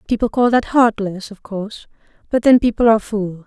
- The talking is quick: No, average, 190 wpm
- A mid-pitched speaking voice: No, high, 215 Hz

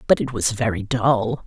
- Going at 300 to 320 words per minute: No, fast, 205 wpm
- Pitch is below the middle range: Yes, low, 115 Hz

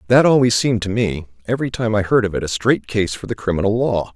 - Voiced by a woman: No, male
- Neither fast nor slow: No, fast, 260 wpm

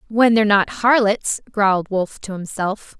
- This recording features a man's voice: No, female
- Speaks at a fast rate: No, average, 180 wpm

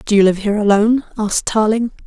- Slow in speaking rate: No, fast, 205 wpm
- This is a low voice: No, high, 210 Hz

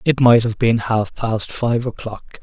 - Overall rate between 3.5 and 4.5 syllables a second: Yes, 3.9 syllables/s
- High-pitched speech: No, low, 115 Hz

